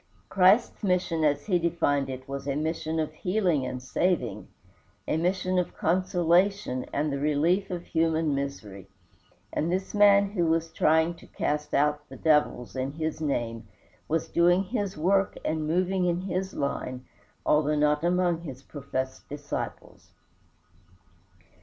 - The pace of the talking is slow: No, average, 145 wpm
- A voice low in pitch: No, medium, 160 Hz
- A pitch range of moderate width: Yes, average, 3.9 semitones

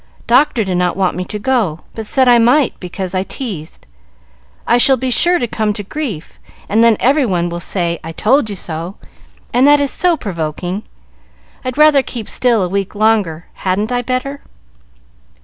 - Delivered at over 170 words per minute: Yes, average, 185 wpm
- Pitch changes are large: Yes, wide, 5.8 semitones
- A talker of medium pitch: No, high, 215 Hz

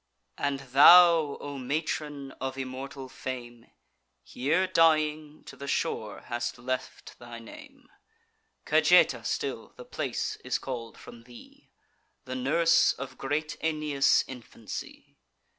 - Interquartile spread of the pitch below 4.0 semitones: Yes, average, 3.5 semitones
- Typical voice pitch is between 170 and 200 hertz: No, medium, 140 Hz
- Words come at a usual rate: No, slow, 115 wpm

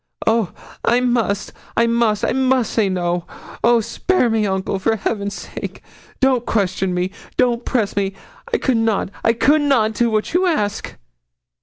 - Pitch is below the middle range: No, high, 225 Hz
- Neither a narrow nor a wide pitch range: Yes, average, 3.4 semitones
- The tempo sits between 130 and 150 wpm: No, average, 165 wpm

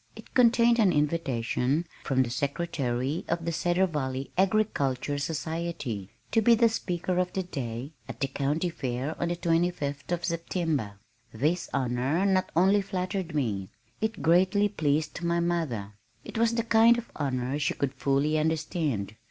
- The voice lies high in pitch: No, medium, 160 Hz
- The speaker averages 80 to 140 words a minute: No, average, 160 wpm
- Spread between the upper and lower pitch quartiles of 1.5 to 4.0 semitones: No, average, 5.1 semitones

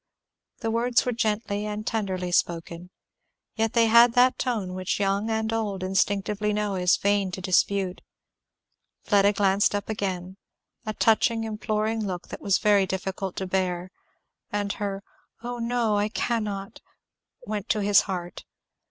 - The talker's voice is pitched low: No, high, 205 Hz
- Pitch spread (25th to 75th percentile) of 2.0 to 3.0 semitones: Yes, narrow, 2.5 semitones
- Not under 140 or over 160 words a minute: Yes, average, 150 wpm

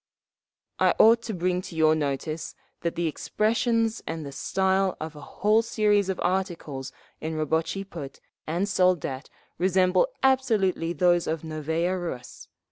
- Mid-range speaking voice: Yes, medium, 175 Hz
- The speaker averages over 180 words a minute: No, average, 140 wpm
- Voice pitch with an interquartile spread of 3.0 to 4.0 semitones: Yes, average, 3.7 semitones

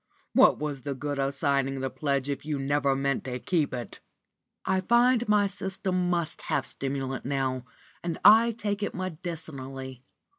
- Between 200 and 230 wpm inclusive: No, average, 160 wpm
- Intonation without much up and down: No, wide, 5.5 semitones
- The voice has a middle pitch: Yes, medium, 145 Hz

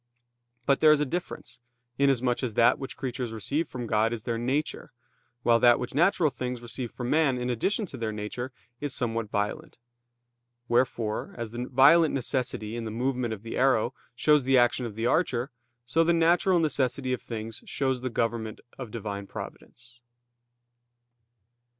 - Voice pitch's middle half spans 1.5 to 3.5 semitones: Yes, average, 3.0 semitones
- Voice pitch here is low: Yes, low, 125 Hz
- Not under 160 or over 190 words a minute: Yes, average, 170 wpm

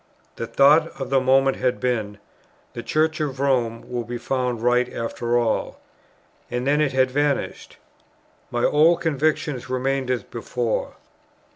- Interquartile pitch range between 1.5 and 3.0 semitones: Yes, average, 2.7 semitones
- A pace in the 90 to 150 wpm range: Yes, average, 145 wpm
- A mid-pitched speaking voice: No, low, 130 Hz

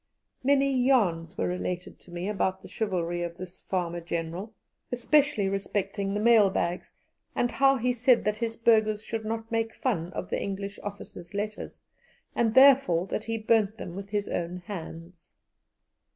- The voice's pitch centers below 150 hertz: No, high, 205 Hz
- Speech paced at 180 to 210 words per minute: No, average, 165 wpm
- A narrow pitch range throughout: No, average, 4.1 semitones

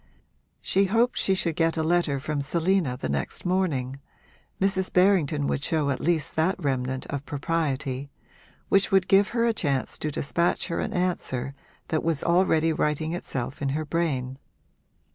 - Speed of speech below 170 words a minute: Yes, average, 160 wpm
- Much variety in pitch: No, average, 4.7 semitones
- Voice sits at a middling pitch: Yes, medium, 160 Hz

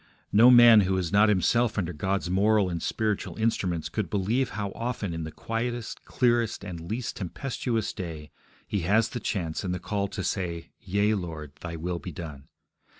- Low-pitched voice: Yes, low, 100 Hz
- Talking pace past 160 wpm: Yes, average, 180 wpm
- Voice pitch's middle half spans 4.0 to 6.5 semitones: Yes, average, 4.5 semitones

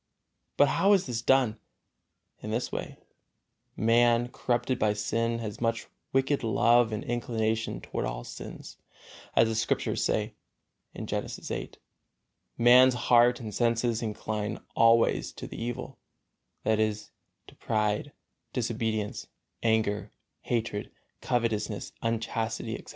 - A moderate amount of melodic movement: No, narrow, 1.8 semitones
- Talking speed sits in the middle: No, slow, 120 wpm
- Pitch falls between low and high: No, low, 115 Hz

